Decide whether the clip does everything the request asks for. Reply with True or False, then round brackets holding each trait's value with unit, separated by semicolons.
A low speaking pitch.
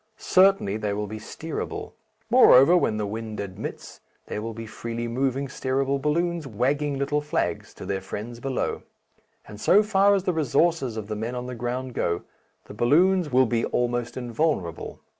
True (125 Hz)